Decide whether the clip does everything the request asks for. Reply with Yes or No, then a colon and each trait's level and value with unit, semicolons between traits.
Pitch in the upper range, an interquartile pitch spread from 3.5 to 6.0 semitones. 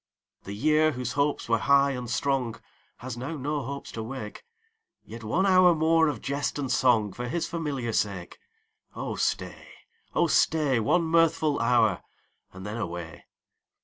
No: low, 135 Hz; average, 5.1 semitones